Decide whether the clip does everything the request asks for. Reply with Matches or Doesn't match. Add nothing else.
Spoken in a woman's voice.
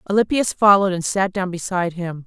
Matches